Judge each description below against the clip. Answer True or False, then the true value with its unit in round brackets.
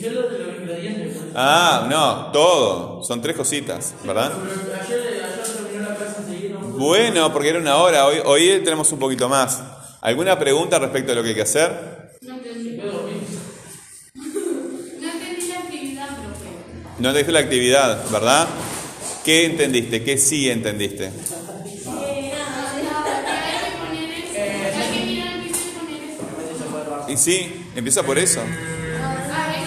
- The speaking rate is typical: False (85 wpm)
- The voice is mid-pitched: False (195 Hz)